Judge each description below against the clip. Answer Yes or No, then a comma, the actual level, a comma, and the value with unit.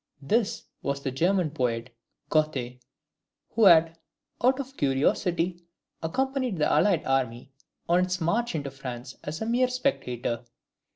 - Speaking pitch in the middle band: Yes, medium, 160 Hz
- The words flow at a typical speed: No, slow, 130 wpm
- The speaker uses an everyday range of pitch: No, wide, 7.6 semitones